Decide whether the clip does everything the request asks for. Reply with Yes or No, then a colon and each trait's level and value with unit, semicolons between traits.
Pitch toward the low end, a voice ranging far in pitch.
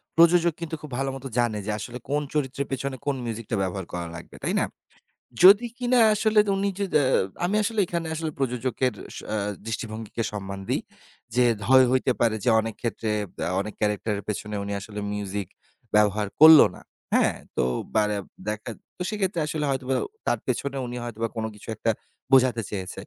Yes: low, 125 Hz; wide, 6.2 semitones